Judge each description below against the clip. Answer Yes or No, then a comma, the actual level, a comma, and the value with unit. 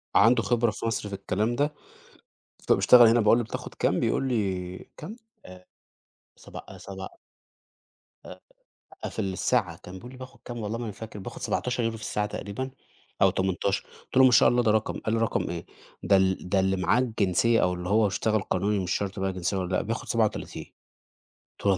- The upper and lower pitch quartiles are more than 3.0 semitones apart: Yes, average, 3.6 semitones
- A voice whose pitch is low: Yes, low, 105 Hz